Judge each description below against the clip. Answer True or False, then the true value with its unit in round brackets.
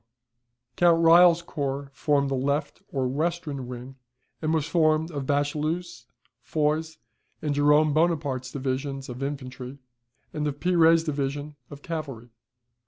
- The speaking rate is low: True (125 wpm)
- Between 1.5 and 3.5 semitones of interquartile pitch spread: True (2.8 semitones)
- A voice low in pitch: False (145 Hz)